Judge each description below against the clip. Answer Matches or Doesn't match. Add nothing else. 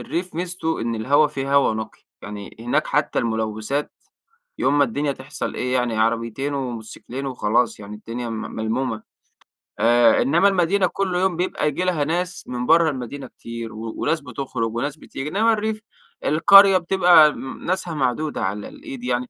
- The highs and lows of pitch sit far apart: Matches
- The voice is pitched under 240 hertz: Matches